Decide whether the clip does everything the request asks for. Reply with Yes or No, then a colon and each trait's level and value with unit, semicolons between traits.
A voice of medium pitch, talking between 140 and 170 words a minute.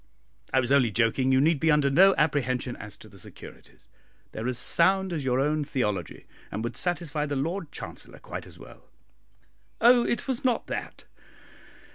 No: medium, 145 Hz; average, 180 wpm